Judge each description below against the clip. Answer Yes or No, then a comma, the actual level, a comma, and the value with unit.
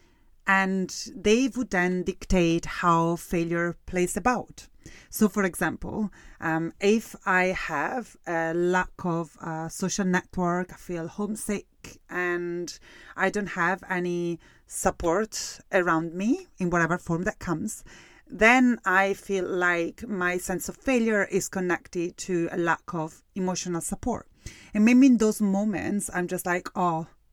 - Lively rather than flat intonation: No, average, 2.7 semitones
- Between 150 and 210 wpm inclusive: No, average, 140 wpm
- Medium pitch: Yes, medium, 180 Hz